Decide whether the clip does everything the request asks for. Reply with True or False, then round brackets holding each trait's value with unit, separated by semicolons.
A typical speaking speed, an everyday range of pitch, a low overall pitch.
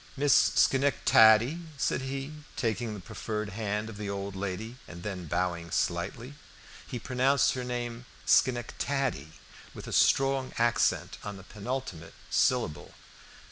False (130 wpm; 4.6 semitones; 115 Hz)